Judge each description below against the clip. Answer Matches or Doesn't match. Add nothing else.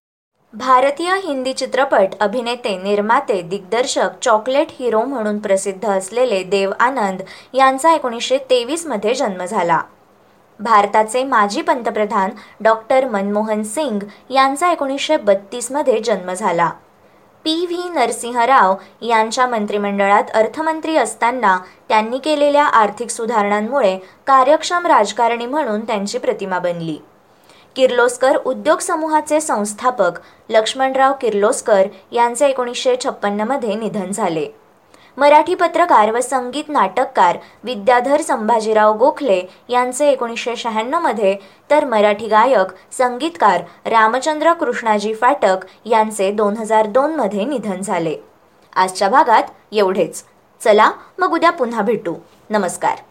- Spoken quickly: Doesn't match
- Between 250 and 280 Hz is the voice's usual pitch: Doesn't match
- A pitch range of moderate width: Matches